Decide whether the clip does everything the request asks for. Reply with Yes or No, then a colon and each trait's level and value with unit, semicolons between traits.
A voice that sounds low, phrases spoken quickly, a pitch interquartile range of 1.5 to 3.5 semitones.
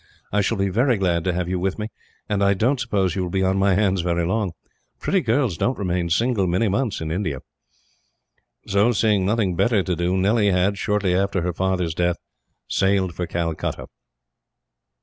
No: very low, 95 Hz; average, 190 wpm; narrow, 2.6 semitones